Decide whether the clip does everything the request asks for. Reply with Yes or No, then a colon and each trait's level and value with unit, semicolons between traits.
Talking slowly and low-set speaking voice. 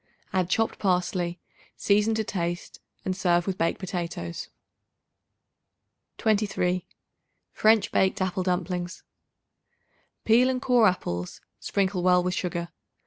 No: slow, 110 wpm; medium, 185 Hz